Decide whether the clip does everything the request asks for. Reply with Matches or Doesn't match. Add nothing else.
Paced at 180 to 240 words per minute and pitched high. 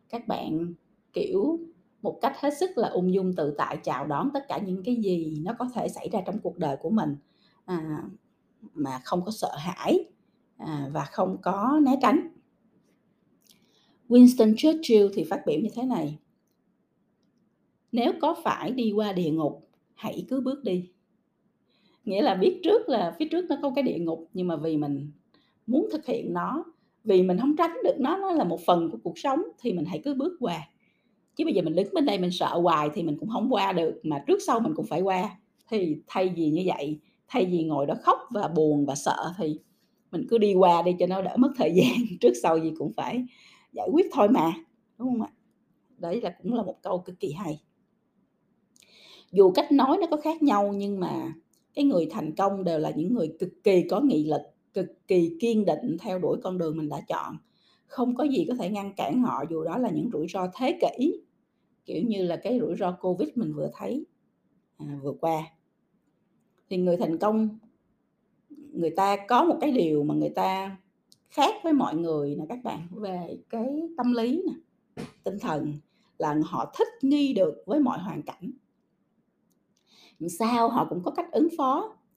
Matches